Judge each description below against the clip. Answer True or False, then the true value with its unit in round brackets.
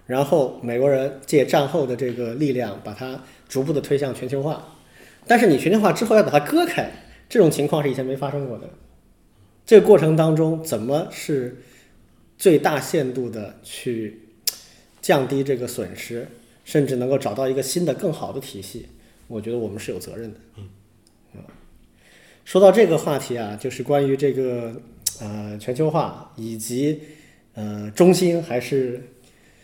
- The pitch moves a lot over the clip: False (4.3 semitones)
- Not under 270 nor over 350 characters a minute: False (240 characters per minute)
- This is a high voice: False (130 Hz)